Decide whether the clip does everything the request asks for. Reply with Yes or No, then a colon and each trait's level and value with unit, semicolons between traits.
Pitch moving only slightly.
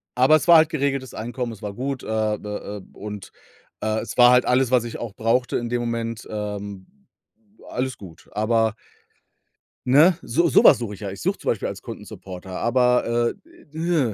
No: average, 3.3 semitones